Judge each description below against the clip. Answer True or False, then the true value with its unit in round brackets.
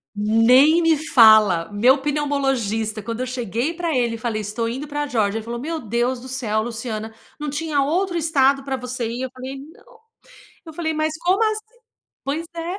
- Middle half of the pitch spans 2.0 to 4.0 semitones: False (5.3 semitones)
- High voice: True (260 Hz)